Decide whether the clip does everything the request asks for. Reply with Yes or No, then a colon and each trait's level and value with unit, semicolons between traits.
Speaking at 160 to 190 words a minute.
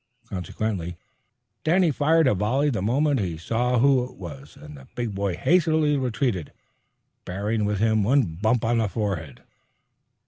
No: average, 150 wpm